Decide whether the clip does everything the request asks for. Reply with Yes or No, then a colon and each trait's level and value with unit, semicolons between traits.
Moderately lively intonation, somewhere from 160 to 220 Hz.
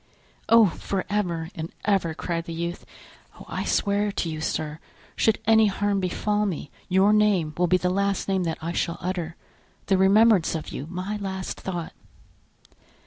Yes: average, 3.3 semitones; medium, 185 Hz